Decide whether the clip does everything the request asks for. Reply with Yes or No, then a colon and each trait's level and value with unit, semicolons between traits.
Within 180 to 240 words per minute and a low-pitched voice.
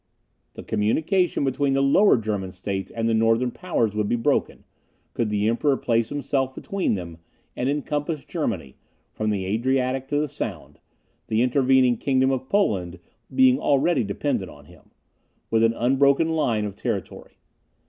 No: average, 155 wpm; low, 125 Hz